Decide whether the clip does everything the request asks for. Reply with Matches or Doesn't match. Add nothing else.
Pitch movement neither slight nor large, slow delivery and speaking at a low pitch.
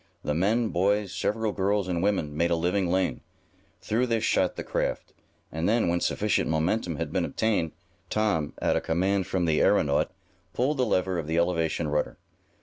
Doesn't match